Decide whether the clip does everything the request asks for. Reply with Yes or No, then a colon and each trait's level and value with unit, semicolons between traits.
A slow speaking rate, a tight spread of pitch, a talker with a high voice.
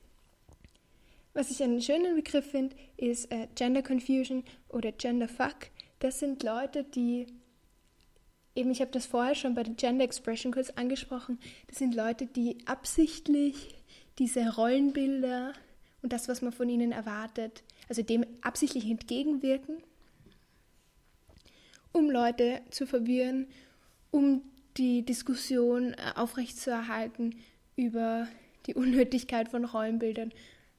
Yes: slow, 115 wpm; narrow, 2.1 semitones; very high, 250 Hz